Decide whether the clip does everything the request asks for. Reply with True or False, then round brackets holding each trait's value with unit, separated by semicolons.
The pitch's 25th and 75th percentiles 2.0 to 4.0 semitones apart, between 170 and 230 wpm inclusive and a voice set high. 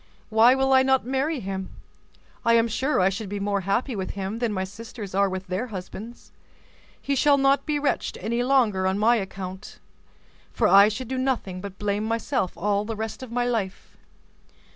False (4.6 semitones; 190 wpm; 220 Hz)